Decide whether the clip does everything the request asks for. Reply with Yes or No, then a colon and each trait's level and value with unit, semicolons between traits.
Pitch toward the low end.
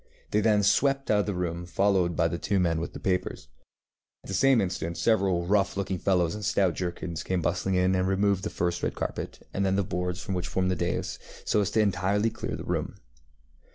Yes: very low, 95 Hz